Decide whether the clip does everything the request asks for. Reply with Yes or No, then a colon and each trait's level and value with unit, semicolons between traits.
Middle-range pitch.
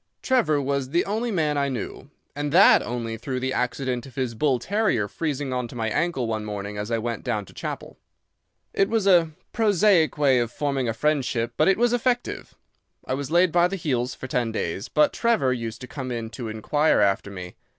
No: low, 130 Hz